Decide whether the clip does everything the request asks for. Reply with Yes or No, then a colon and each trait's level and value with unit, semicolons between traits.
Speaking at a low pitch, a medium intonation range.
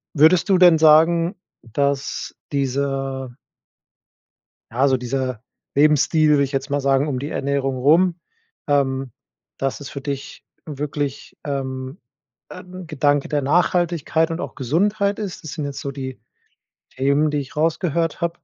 No: medium, 145 Hz; average, 3.2 semitones